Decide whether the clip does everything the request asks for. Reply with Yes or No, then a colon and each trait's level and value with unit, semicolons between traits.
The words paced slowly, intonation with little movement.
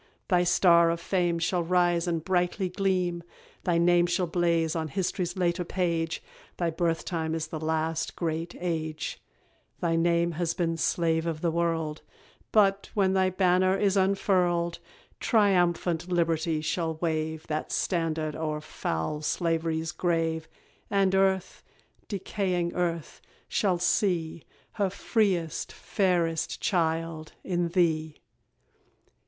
Yes: slow, 125 wpm; narrow, 2.0 semitones